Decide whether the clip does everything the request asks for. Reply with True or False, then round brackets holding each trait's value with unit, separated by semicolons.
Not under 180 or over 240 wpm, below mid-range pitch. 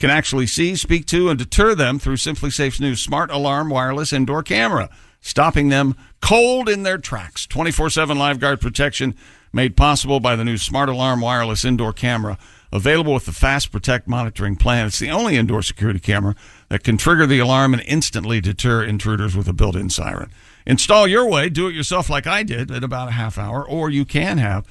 True (200 wpm; 130 Hz)